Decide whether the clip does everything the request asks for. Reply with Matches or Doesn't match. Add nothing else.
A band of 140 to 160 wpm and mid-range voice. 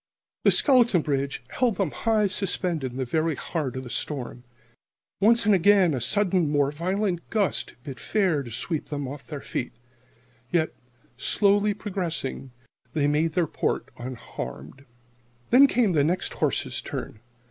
Matches